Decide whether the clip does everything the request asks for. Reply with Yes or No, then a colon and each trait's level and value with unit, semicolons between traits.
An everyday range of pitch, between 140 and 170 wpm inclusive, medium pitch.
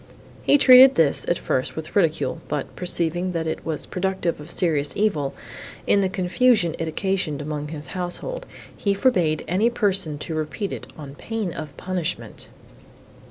Yes: average, 4.2 semitones; average, 160 wpm; medium, 175 Hz